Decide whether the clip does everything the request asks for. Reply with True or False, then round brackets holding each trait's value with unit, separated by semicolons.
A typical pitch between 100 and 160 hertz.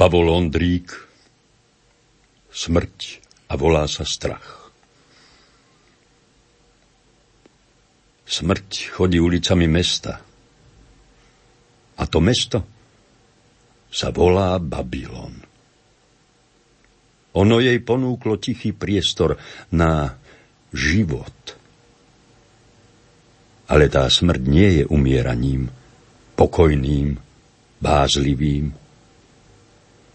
False (90 Hz)